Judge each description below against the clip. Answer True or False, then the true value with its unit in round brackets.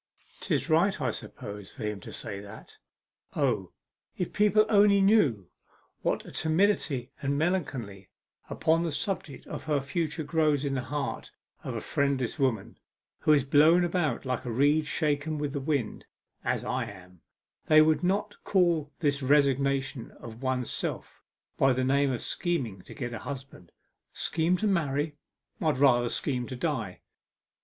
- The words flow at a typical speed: True (160 wpm)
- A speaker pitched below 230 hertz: True (140 Hz)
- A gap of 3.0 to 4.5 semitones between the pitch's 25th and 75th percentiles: True (4.1 semitones)